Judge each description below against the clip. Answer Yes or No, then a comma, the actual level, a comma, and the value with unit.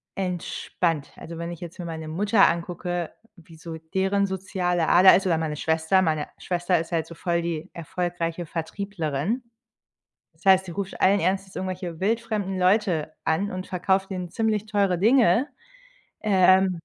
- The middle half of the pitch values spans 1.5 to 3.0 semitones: Yes, narrow, 2.6 semitones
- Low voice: No, medium, 180 Hz